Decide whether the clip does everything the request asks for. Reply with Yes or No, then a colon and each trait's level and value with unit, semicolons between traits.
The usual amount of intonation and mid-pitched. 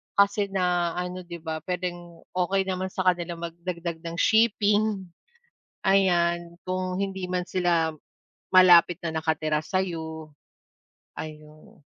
No: narrow, 1.9 semitones; medium, 175 Hz